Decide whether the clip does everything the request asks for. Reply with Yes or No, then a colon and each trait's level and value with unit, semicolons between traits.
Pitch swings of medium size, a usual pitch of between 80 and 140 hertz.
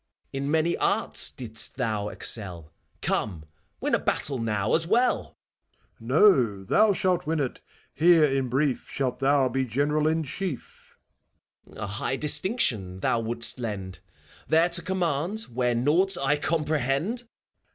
No: wide, 6.2 semitones; low, 135 Hz